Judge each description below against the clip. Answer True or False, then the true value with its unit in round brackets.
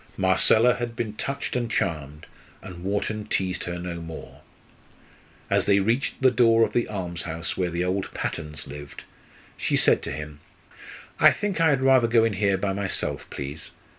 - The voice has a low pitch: True (100 Hz)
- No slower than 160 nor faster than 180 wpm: True (170 wpm)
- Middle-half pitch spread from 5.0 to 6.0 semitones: True (5.3 semitones)